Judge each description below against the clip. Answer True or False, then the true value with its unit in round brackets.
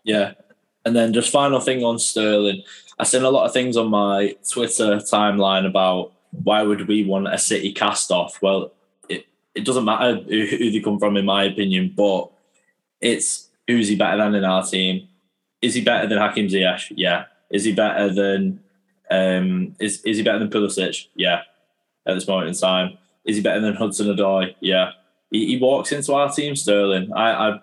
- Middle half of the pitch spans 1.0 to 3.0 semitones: True (2.4 semitones)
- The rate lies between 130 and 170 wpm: False (190 wpm)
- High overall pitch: False (105 Hz)